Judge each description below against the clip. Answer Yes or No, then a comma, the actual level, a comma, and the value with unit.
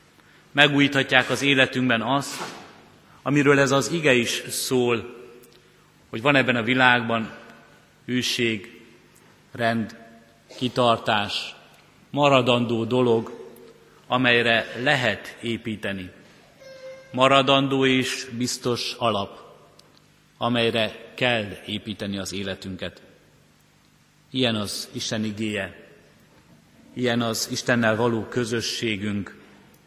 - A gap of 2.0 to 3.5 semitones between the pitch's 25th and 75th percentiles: Yes, narrow, 2.4 semitones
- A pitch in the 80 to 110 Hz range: No, low, 120 Hz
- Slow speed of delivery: Yes, slow, 80 wpm